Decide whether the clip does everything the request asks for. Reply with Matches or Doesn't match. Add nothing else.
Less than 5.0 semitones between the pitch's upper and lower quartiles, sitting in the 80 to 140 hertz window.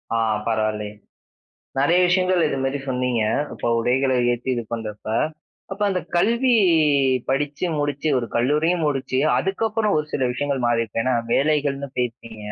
Doesn't match